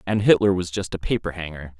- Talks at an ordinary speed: No, fast, 235 wpm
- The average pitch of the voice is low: Yes, very low, 90 Hz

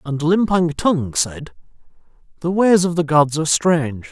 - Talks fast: No, average, 160 wpm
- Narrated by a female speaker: No, male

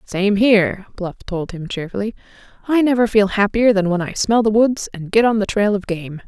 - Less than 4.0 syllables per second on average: No, 5.2 syllables/s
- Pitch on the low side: No, high, 205 Hz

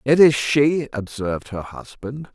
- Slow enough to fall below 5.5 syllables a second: Yes, 4.2 syllables/s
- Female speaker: No, male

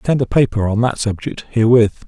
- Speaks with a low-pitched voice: Yes, low, 120 Hz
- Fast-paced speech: Yes, fast, 230 wpm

